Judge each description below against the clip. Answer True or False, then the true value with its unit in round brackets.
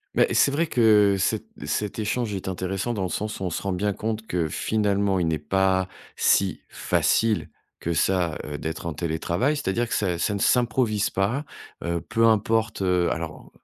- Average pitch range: True (3.8 semitones)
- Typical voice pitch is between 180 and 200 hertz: False (100 Hz)